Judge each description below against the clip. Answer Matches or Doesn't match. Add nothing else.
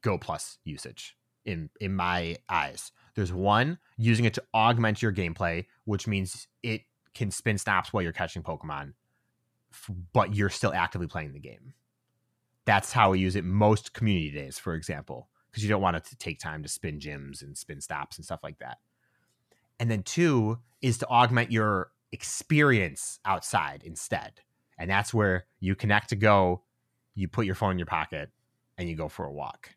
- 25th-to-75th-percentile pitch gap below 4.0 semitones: Doesn't match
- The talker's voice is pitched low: Matches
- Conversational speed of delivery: Matches